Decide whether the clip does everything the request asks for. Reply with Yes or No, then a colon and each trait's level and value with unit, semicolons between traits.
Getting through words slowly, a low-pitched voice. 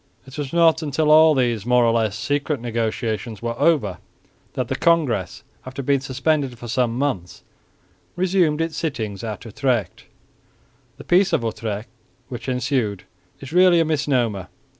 No: average, 150 wpm; low, 130 Hz